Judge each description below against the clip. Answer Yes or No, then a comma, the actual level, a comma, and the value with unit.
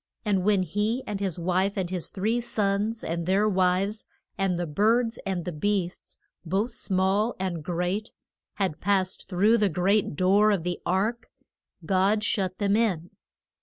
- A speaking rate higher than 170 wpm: No, average, 160 wpm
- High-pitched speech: Yes, high, 195 Hz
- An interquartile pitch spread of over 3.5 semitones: No, narrow, 2.6 semitones